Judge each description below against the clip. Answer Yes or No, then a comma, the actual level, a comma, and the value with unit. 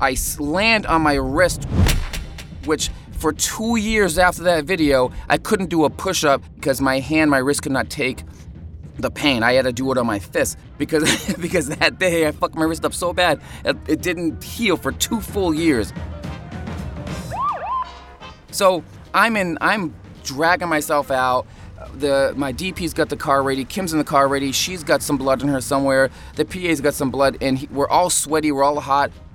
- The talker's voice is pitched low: No, medium, 145 Hz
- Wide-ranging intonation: No, average, 4.3 semitones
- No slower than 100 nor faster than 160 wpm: No, average, 185 wpm